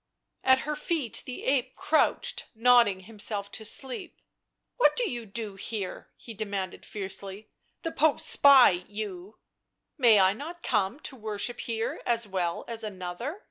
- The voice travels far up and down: No, average, 4.6 semitones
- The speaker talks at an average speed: Yes, average, 170 wpm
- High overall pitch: Yes, high, 220 Hz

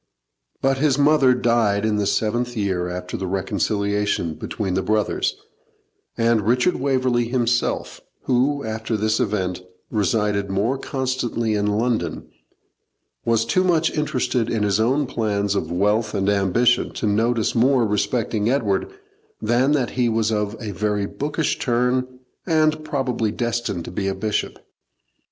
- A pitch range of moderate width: Yes, average, 3.6 semitones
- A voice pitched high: No, low, 115 Hz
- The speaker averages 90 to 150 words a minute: Yes, average, 140 wpm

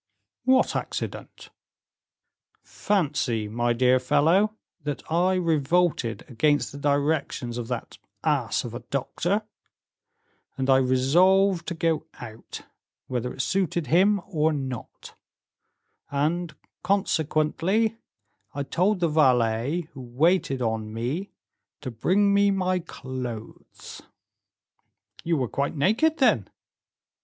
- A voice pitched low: No, medium, 150 Hz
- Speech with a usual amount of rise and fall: No, wide, 6.3 semitones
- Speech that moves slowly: Yes, slow, 110 wpm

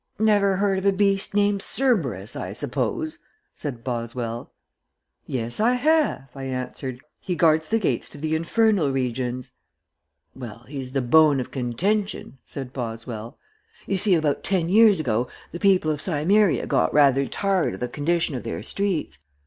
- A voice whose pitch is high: No, medium, 155 Hz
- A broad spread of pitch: Yes, wide, 7.7 semitones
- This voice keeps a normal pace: Yes, average, 155 wpm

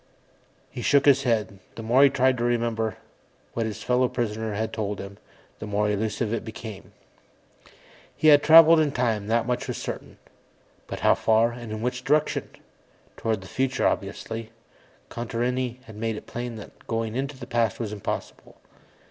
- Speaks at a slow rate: No, average, 170 wpm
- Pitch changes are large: No, narrow, 2.4 semitones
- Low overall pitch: Yes, low, 115 Hz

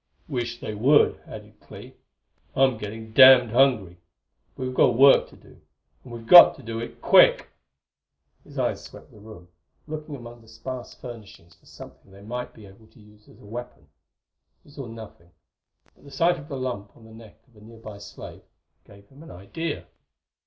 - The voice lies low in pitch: Yes, low, 115 Hz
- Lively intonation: No, average, 3.6 semitones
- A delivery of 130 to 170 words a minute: No, average, 185 wpm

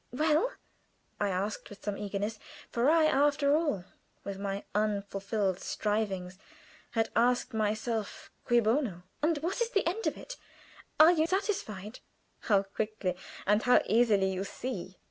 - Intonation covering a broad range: Yes, wide, 6.5 semitones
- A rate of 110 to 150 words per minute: Yes, average, 140 wpm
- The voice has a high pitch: Yes, high, 215 Hz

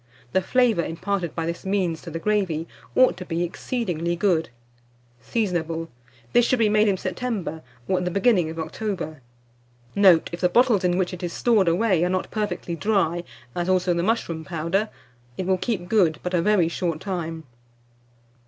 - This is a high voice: No, medium, 180 Hz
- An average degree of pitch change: Yes, average, 3.5 semitones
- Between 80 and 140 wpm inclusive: No, average, 180 wpm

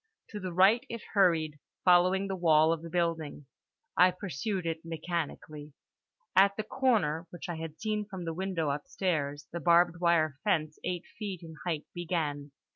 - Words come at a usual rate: Yes, average, 165 wpm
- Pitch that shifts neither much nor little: Yes, average, 3.2 semitones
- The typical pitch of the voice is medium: Yes, medium, 170 Hz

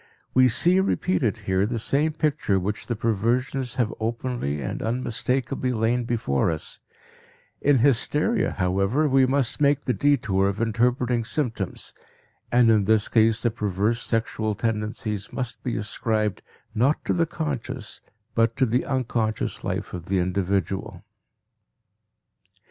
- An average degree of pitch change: Yes, average, 3.6 semitones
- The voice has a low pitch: Yes, low, 115 Hz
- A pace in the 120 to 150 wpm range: Yes, slow, 135 wpm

